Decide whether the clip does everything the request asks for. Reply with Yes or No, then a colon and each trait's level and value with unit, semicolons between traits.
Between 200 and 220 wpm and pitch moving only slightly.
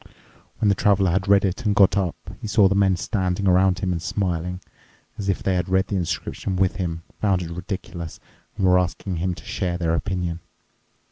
Yes: fast, 205 wpm; narrow, 1.7 semitones